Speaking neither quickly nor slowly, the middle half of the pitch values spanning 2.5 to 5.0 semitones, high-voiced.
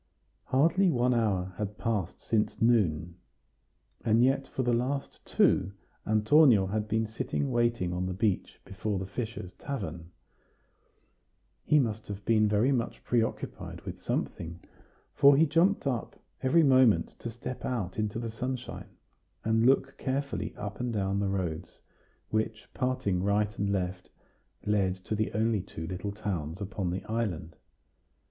No: average, 145 wpm; average, 4.3 semitones; low, 110 Hz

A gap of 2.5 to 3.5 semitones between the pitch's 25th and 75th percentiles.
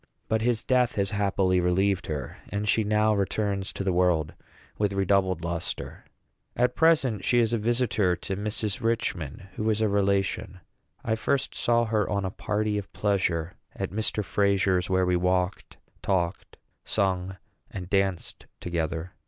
Yes: average, 2.9 semitones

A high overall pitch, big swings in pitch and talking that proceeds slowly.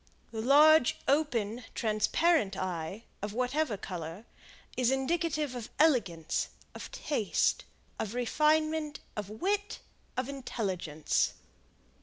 Yes: high, 245 Hz; wide, 6.9 semitones; slow, 100 wpm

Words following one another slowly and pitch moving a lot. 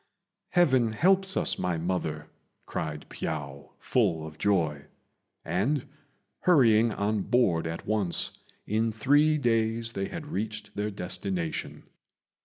Yes: slow, 115 wpm; wide, 6.1 semitones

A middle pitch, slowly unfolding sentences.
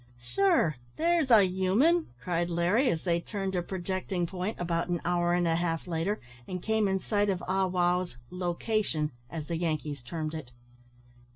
No: medium, 180 Hz; average, 175 wpm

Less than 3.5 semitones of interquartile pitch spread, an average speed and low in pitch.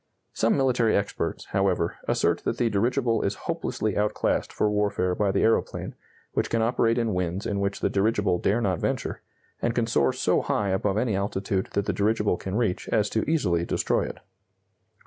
Yes: average, 2.8 semitones; average, 185 wpm; low, 105 Hz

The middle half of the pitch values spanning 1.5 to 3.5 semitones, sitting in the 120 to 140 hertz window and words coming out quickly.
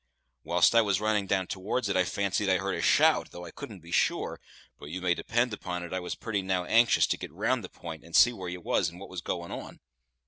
No: average, 2.7 semitones; very low, 95 Hz; fast, 255 wpm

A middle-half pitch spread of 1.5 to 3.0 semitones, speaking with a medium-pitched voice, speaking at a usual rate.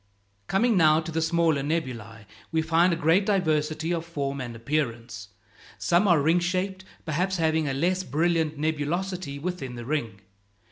No: average, 3.7 semitones; medium, 160 Hz; average, 155 wpm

